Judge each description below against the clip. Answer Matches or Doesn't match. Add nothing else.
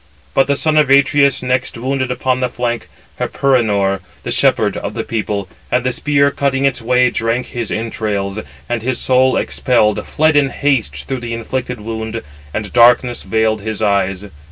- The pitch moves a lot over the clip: Doesn't match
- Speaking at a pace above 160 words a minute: Matches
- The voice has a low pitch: Matches